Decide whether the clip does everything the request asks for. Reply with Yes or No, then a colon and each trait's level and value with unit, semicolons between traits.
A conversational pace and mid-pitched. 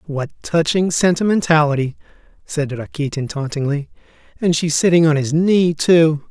No: slow, 125 wpm; medium, 155 Hz